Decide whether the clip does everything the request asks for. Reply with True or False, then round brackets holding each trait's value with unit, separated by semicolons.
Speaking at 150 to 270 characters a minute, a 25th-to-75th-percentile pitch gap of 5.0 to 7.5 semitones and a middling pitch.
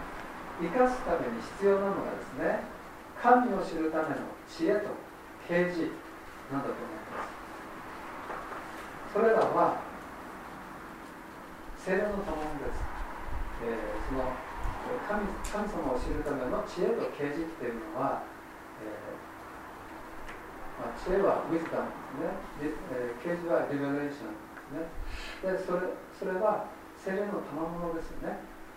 True (245 characters per minute; 5.3 semitones; 170 Hz)